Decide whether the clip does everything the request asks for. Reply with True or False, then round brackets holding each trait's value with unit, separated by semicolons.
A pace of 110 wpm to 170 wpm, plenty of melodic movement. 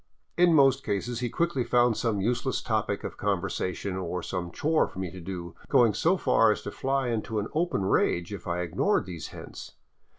False (195 wpm; 6.2 semitones)